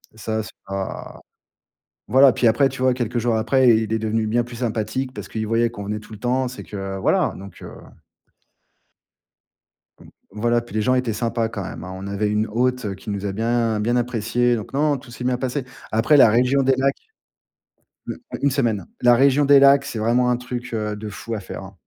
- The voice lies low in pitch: Yes, low, 115 Hz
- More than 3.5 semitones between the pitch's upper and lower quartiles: No, average, 2.8 semitones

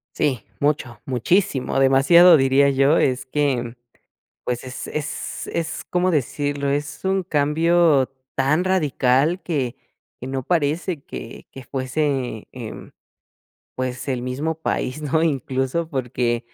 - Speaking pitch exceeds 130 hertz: Yes, medium, 140 Hz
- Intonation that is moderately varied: Yes, average, 3.7 semitones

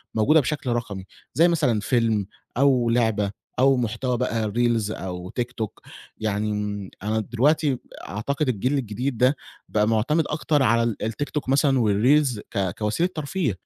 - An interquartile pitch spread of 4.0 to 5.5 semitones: Yes, average, 4.6 semitones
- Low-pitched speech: Yes, low, 120 Hz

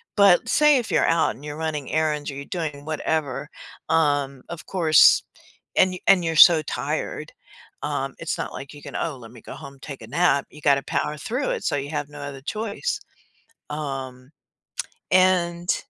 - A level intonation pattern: No, average, 3.6 semitones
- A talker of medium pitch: Yes, medium, 150 Hz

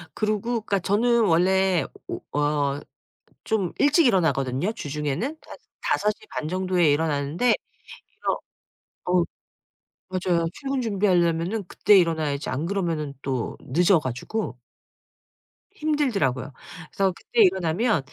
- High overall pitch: No, medium, 180 Hz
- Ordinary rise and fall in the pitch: No, wide, 5.8 semitones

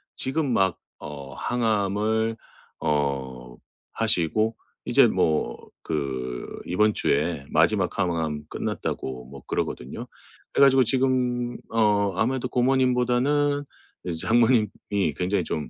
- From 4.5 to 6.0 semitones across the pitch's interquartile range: No, wide, 8.2 semitones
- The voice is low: Yes, low, 105 Hz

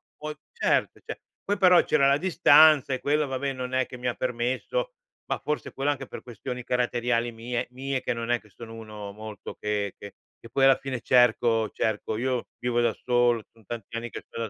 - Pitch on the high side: No, low, 125 Hz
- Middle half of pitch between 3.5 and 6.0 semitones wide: No, average, 2.7 semitones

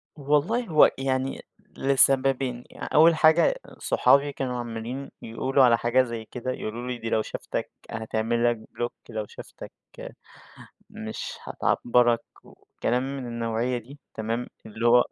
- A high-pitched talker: No, low, 125 Hz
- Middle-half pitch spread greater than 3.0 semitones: No, average, 2.7 semitones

